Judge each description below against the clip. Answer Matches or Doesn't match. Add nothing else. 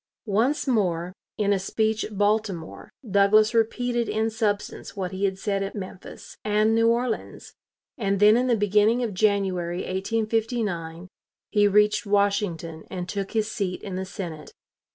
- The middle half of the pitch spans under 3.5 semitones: Matches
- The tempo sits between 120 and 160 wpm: Matches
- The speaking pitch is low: Doesn't match